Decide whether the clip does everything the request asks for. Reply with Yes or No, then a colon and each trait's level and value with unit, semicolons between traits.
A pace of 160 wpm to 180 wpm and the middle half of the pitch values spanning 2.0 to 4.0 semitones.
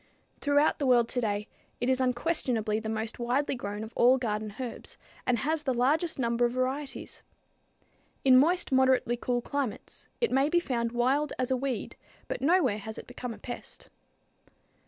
Yes: average, 170 wpm; average, 2.9 semitones